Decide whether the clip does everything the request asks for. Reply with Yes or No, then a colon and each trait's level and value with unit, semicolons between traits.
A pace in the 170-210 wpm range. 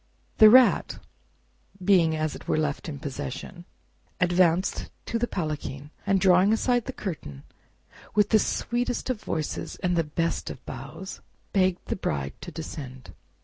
No: average, 145 wpm